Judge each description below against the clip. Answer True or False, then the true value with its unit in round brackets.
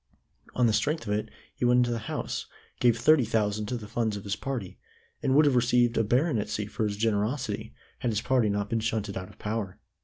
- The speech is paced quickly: True (220 wpm)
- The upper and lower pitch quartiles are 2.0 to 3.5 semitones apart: True (2.9 semitones)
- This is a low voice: True (115 Hz)